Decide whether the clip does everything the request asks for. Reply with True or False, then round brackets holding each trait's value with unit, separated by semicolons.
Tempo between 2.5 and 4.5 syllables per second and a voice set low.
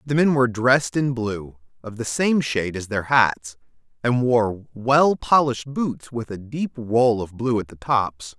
True (4.2 syllables/s; 120 Hz)